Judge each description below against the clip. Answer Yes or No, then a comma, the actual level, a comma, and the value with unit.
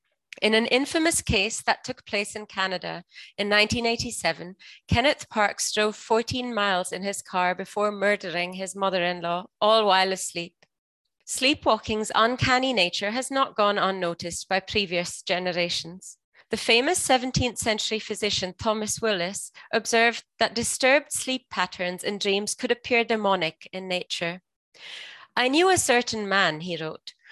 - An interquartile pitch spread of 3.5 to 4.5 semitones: Yes, average, 4.2 semitones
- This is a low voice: No, high, 205 Hz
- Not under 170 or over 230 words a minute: No, average, 140 wpm